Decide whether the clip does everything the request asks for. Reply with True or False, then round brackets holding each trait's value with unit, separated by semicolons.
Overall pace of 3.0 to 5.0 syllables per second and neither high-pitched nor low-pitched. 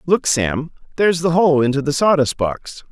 True (4.8 syllables/s; 150 Hz)